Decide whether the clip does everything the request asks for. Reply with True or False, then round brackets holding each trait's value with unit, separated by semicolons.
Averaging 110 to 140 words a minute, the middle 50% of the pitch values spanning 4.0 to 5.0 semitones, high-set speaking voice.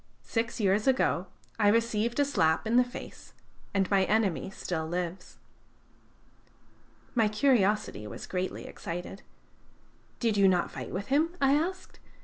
True (135 wpm; 4.3 semitones; 210 Hz)